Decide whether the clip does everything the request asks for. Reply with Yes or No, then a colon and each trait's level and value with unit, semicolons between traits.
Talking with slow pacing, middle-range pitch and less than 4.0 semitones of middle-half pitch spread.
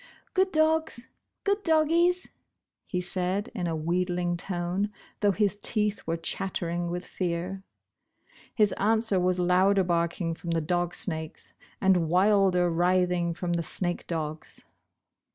Yes: slow, 130 wpm; medium, 180 Hz; average, 2.9 semitones